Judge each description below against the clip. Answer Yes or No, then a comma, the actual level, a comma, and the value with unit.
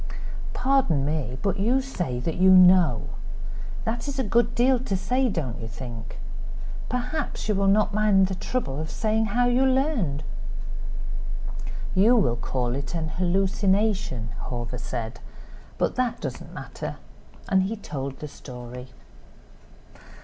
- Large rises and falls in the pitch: Yes, wide, 9.0 semitones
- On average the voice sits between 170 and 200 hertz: Yes, high, 190 Hz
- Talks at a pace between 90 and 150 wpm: Yes, average, 140 wpm